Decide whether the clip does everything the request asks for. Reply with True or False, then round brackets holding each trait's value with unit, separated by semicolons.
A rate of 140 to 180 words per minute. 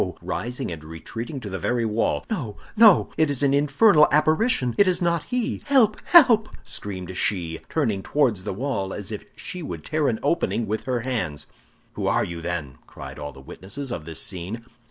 False (190 wpm)